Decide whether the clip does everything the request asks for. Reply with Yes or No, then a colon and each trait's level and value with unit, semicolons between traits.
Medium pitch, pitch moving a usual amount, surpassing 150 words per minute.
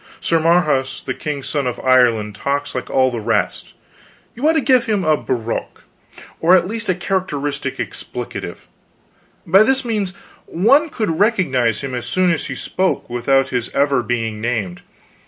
No: medium, 145 Hz; wide, 7.0 semitones; average, 165 wpm